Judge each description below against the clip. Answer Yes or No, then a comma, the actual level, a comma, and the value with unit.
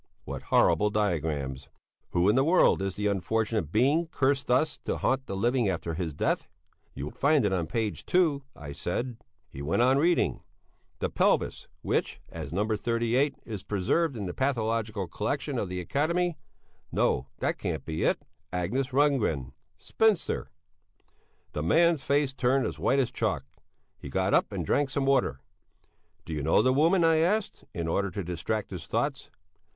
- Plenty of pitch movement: Yes, wide, 7.7 semitones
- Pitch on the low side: Yes, low, 115 Hz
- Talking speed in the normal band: Yes, average, 170 wpm